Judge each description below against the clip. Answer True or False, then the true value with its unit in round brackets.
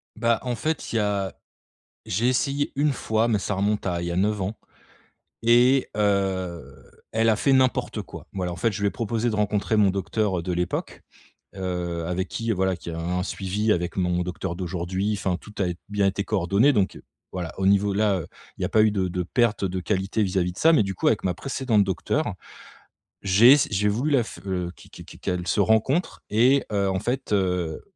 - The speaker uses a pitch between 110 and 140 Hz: False (100 Hz)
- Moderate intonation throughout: True (3.5 semitones)